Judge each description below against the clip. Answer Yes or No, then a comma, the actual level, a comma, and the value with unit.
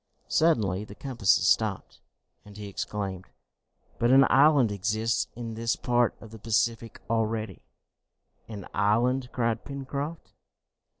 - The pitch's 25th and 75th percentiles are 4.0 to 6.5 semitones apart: No, average, 3.0 semitones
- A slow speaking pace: Yes, slow, 120 wpm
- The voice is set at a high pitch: No, low, 115 Hz